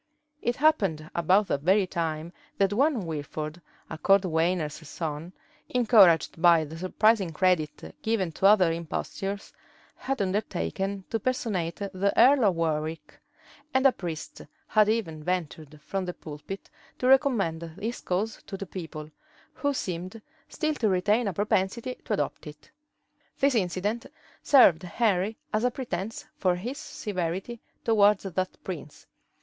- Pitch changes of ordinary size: Yes, average, 4.9 semitones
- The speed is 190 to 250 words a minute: No, average, 140 wpm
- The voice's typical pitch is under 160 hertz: No, high, 190 Hz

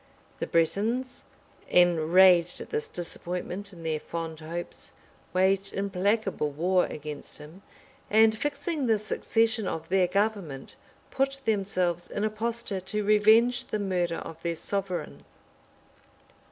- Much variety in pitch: No, average, 4.3 semitones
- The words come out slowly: Yes, slow, 125 wpm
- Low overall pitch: No, high, 195 Hz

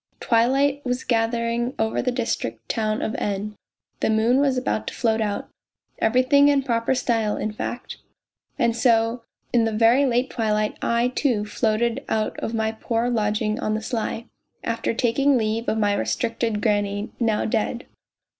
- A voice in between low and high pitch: No, high, 230 Hz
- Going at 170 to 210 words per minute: No, average, 160 wpm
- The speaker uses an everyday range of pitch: No, narrow, 2.2 semitones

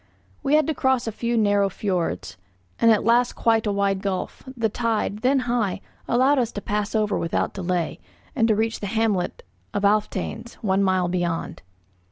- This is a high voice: Yes, high, 210 Hz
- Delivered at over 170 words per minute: Yes, average, 180 wpm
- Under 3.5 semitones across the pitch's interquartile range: Yes, average, 3.1 semitones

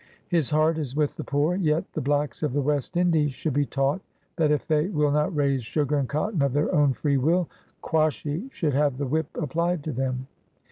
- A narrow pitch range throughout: Yes, narrow, 2.2 semitones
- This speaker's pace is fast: Yes, fast, 220 wpm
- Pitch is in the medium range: Yes, medium, 150 Hz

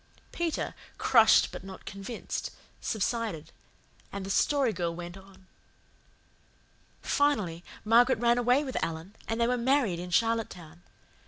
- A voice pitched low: No, high, 220 Hz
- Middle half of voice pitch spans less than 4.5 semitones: No, average, 5.3 semitones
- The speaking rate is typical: No, slow, 130 wpm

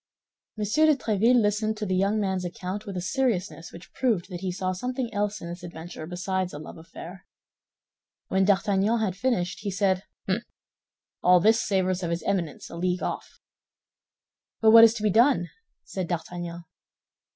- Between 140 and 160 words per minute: No, average, 175 wpm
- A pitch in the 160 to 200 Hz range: Yes, high, 190 Hz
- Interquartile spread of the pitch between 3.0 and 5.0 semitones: Yes, average, 3.3 semitones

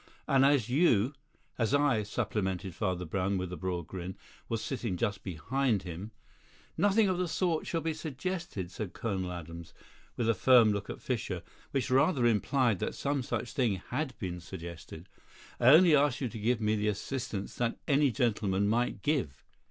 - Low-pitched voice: Yes, low, 115 Hz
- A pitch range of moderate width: No, wide, 6.4 semitones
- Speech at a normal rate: Yes, average, 180 wpm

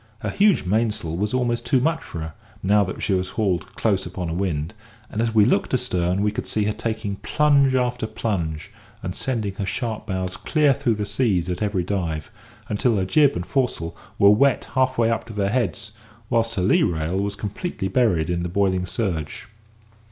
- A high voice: No, low, 105 Hz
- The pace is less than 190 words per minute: No, average, 200 wpm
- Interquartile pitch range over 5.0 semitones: No, average, 4.4 semitones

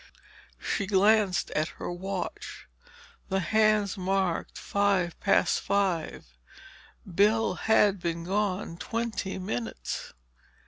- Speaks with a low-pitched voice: No, high, 195 Hz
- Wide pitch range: No, average, 2.8 semitones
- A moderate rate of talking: No, slow, 95 wpm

